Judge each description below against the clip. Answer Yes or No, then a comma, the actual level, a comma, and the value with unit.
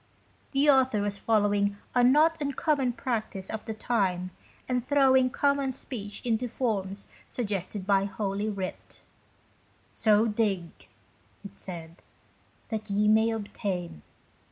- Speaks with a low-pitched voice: No, high, 215 Hz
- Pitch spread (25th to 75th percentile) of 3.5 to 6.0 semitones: Yes, average, 4.1 semitones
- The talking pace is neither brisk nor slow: No, slow, 130 wpm